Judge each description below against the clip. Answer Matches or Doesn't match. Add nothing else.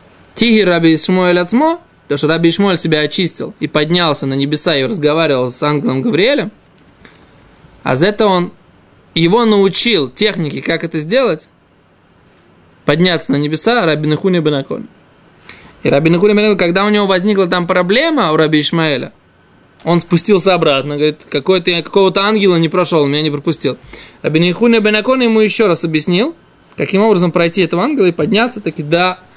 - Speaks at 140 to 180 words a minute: Matches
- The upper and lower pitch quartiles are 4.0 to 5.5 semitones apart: Matches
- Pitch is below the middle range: Doesn't match